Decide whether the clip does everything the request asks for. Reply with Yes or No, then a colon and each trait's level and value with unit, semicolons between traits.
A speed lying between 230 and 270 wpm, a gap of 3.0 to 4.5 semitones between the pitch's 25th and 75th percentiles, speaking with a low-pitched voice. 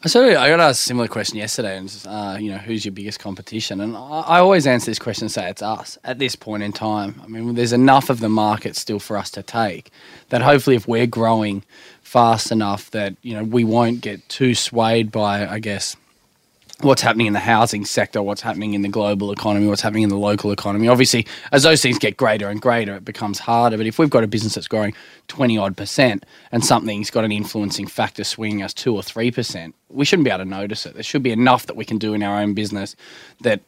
No: fast, 240 wpm; narrow, 2.6 semitones; low, 110 Hz